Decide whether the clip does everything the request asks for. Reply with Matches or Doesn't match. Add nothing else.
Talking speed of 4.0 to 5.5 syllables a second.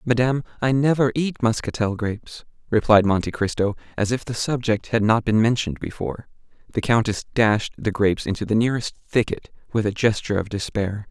Doesn't match